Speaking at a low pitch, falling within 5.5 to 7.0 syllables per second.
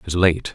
Yes: very low, 85 Hz; 5.9 syllables/s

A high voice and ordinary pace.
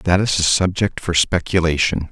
No: very low, 85 Hz; average, 170 wpm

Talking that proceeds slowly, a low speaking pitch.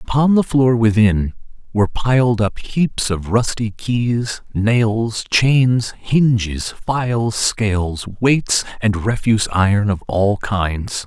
Yes: slow, 125 wpm; low, 110 Hz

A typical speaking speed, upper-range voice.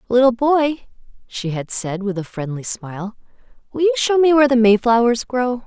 Yes: average, 180 wpm; high, 235 Hz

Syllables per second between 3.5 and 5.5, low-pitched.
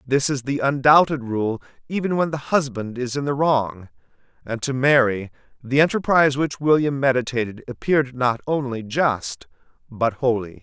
Yes: 4.9 syllables/s; low, 130 Hz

